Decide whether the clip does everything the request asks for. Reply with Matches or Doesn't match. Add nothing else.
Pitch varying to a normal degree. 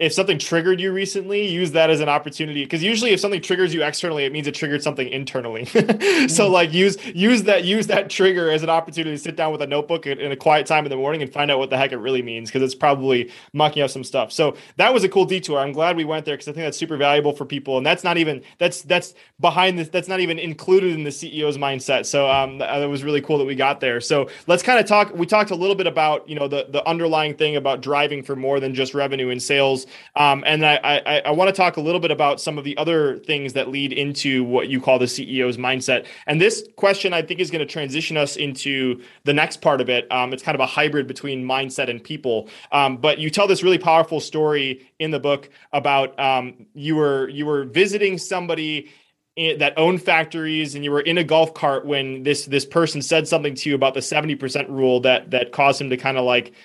Matches